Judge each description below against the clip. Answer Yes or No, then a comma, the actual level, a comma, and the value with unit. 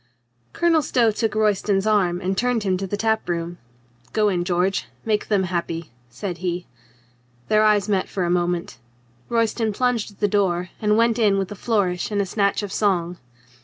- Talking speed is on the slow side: No, average, 185 wpm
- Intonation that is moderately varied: Yes, average, 3.3 semitones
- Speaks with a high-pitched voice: Yes, high, 200 Hz